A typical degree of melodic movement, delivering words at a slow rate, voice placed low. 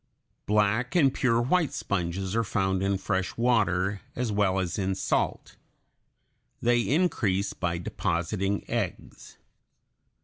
Yes: average, 3.9 semitones; slow, 115 wpm; low, 100 Hz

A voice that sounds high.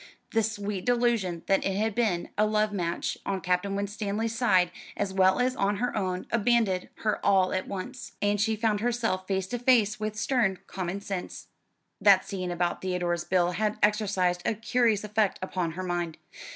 Yes: high, 200 Hz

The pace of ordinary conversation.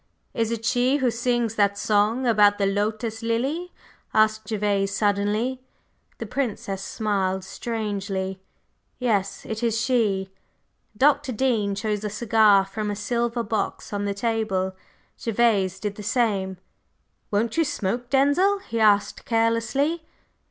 No: slow, 130 wpm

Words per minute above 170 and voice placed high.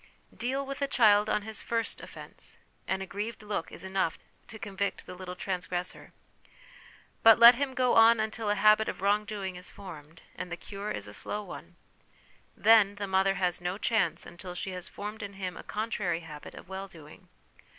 Yes: average, 190 wpm; high, 200 Hz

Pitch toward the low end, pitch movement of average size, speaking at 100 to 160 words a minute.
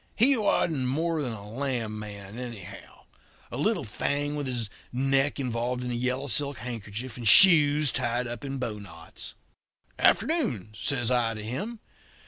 Yes: low, 125 Hz; average, 4.1 semitones; average, 150 wpm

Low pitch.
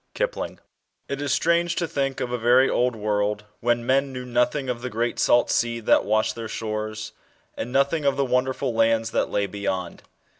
Yes: low, 120 Hz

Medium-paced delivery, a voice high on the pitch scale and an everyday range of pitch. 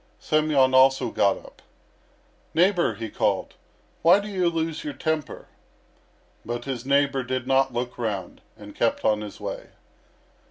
No: average, 145 wpm; low, 135 Hz; average, 4.6 semitones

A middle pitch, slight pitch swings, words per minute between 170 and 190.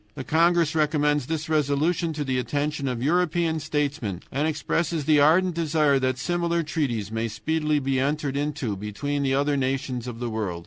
No: medium, 145 Hz; average, 3.4 semitones; average, 175 wpm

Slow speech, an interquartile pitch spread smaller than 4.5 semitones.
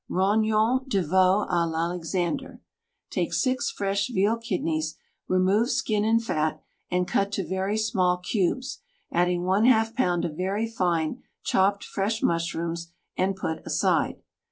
Yes: slow, 130 wpm; average, 3.7 semitones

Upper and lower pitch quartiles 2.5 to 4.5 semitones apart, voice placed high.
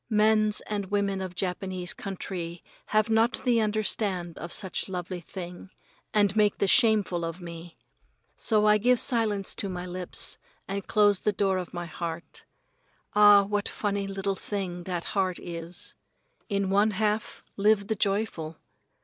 Yes: average, 2.8 semitones; high, 195 Hz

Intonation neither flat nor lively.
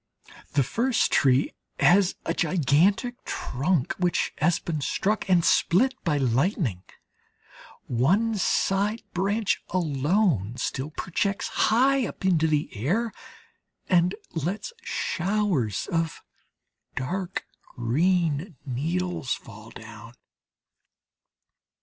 No: wide, 6.4 semitones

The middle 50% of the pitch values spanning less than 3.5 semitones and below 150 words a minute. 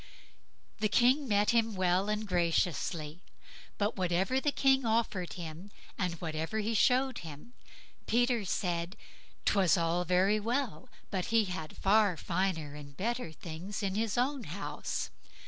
No: average, 4.8 semitones; average, 140 wpm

